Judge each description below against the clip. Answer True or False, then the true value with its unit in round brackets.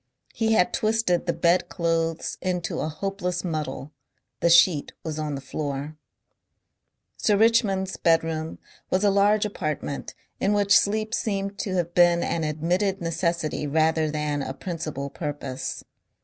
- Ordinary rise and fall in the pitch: True (4.1 semitones)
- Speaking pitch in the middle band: True (170 Hz)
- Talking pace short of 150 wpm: True (140 wpm)